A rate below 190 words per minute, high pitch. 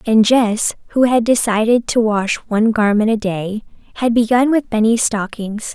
Yes: average, 165 wpm; high, 225 Hz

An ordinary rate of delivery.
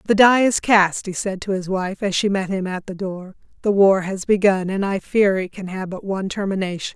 No: fast, 250 wpm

